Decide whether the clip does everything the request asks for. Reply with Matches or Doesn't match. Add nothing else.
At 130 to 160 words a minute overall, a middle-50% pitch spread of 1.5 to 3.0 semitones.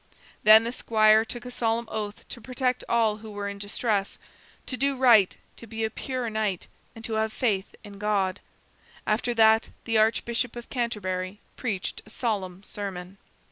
Doesn't match